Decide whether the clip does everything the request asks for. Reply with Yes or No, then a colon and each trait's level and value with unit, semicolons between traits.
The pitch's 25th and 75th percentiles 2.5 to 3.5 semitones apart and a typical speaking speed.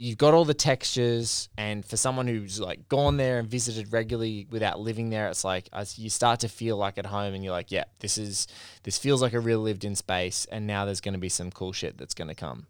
No: average, 2.9 semitones; fast, 260 wpm